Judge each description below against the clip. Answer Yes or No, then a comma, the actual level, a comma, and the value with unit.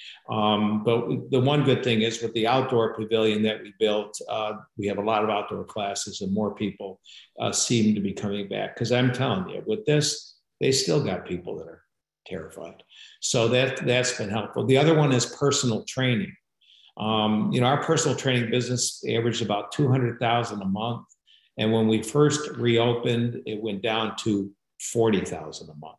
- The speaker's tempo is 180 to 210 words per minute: Yes, average, 190 wpm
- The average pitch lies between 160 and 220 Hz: No, low, 115 Hz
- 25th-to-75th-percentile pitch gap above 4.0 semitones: No, average, 2.8 semitones